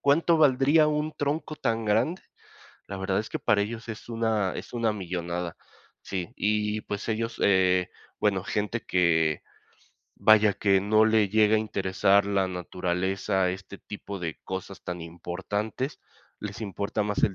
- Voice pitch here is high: No, low, 105 Hz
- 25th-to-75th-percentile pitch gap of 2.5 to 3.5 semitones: Yes, average, 2.9 semitones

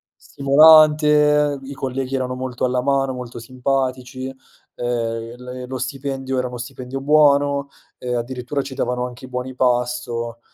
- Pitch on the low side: Yes, low, 130 Hz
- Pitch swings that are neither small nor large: No, narrow, 1.8 semitones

